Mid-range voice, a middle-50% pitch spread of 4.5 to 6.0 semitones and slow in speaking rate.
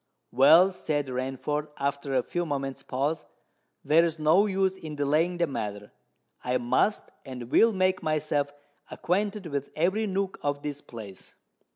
No: medium, 150 Hz; average, 4.9 semitones; average, 145 wpm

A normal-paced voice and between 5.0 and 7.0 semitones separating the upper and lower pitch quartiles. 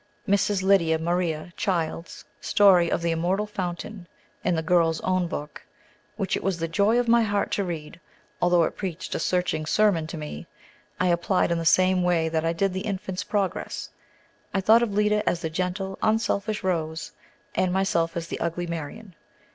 No: average, 180 wpm; average, 3.1 semitones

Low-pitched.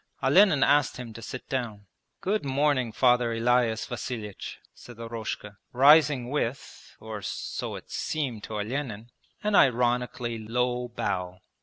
Yes: low, 120 Hz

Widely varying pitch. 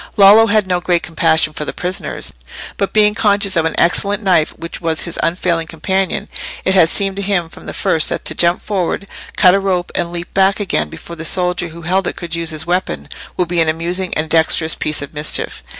No: average, 2.9 semitones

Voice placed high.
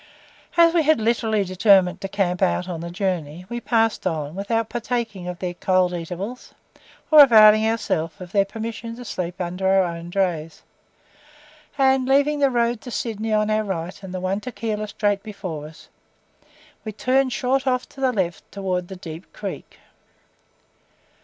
Yes: high, 205 Hz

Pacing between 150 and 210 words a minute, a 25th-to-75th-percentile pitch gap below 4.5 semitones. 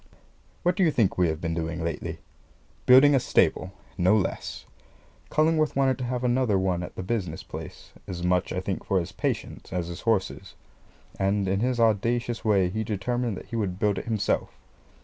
No: average, 190 wpm; average, 4.9 semitones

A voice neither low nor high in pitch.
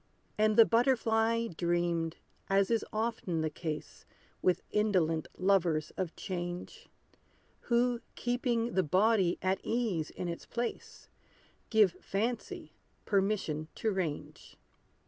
No: high, 195 Hz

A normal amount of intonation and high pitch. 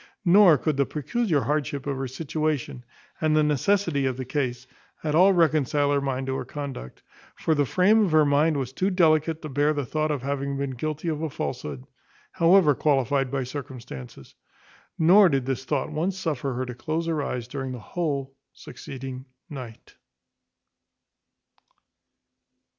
No: average, 3.0 semitones; medium, 145 Hz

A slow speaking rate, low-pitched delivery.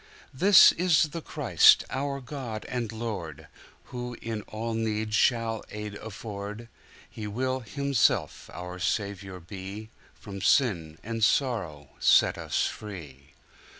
Yes: slow, 110 wpm; low, 110 Hz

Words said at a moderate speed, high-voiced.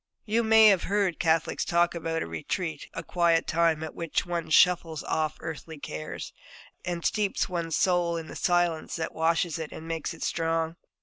No: average, 180 wpm; medium, 165 Hz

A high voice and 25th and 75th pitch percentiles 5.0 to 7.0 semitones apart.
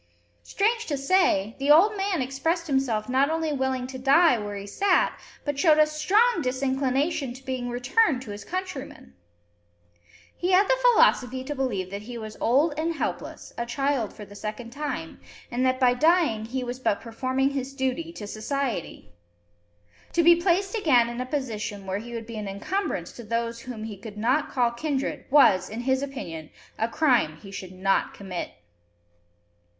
Yes: very high, 260 Hz; average, 5.3 semitones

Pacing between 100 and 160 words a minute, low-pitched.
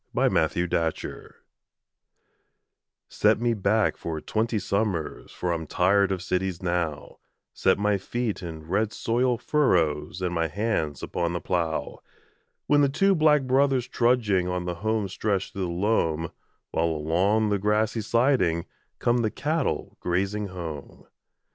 Yes: average, 150 wpm; very low, 95 Hz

